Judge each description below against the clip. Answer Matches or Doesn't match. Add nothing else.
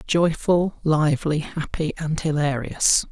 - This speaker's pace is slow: Matches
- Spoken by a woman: Doesn't match